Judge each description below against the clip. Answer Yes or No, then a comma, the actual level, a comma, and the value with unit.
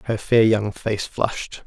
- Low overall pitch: Yes, low, 105 Hz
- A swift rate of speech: No, average, 180 wpm